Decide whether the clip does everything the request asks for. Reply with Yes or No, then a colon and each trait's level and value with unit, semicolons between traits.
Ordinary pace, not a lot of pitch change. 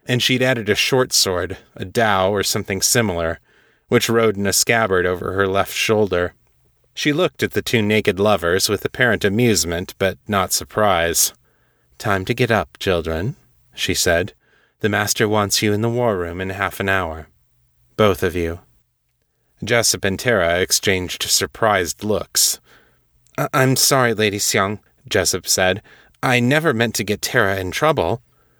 No: average, 155 wpm; average, 4.0 semitones